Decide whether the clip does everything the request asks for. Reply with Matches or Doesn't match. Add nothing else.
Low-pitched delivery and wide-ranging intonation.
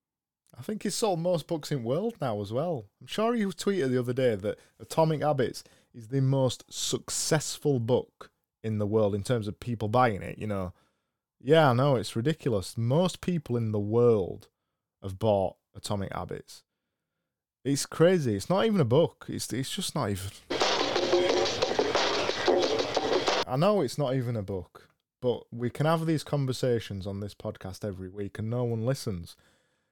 Matches